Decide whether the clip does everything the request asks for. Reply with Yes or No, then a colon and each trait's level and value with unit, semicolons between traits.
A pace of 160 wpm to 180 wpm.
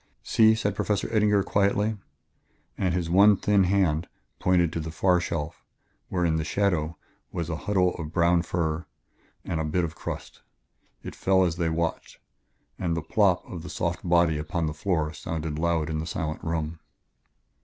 Yes: average, 175 wpm